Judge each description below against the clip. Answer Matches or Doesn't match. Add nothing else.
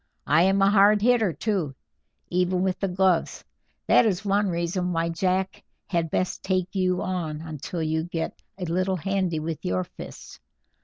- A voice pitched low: Doesn't match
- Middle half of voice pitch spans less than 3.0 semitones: Matches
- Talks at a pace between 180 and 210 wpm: Doesn't match